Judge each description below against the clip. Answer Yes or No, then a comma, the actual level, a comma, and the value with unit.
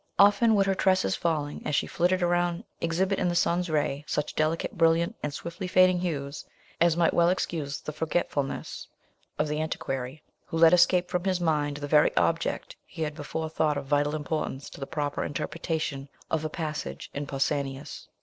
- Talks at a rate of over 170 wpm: Yes, average, 180 wpm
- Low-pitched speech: No, medium, 160 Hz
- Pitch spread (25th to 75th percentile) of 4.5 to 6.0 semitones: No, average, 3.1 semitones